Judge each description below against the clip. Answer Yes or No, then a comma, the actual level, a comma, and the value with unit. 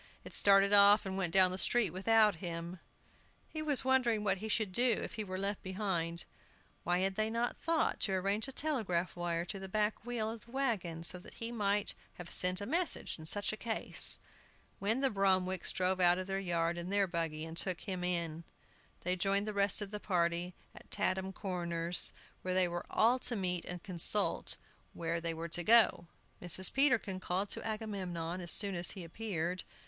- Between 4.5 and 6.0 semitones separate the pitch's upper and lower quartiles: No, average, 3.5 semitones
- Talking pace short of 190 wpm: No, average, 200 wpm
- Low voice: No, high, 190 Hz